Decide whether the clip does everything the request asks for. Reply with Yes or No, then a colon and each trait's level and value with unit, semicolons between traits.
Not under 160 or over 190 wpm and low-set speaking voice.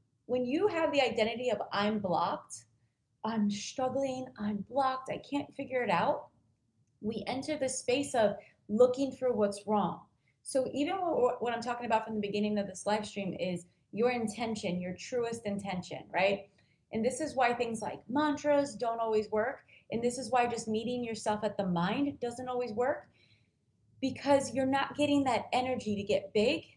No: average, 175 wpm; high, 235 Hz